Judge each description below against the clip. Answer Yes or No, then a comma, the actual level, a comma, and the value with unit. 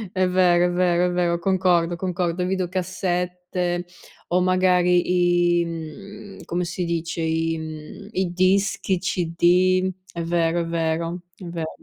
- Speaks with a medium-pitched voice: Yes, medium, 175 Hz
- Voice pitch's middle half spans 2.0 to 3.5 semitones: No, narrow, 1.5 semitones